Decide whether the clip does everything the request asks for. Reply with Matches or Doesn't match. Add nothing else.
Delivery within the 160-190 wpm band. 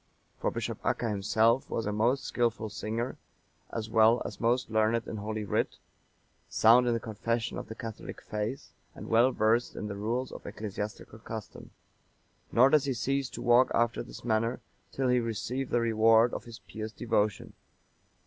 Matches